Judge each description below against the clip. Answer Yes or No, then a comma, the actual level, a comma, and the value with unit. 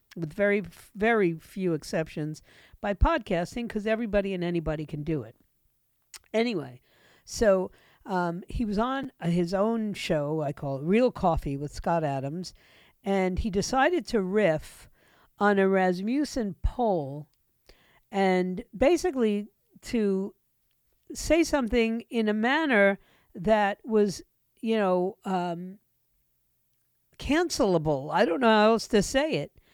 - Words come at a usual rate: No, slow, 125 wpm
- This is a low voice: No, high, 195 Hz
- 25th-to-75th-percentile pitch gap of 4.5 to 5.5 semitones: Yes, average, 5.1 semitones